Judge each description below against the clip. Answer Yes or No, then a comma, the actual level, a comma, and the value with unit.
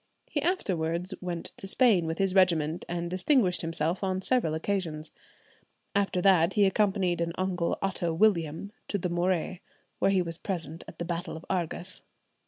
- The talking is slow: No, average, 165 wpm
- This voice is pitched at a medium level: Yes, medium, 180 Hz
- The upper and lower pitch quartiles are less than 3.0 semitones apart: Yes, narrow, 2.6 semitones